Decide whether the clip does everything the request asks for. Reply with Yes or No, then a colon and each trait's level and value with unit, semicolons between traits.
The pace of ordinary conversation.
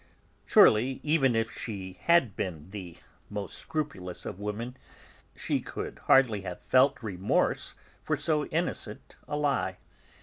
No: slow, 125 wpm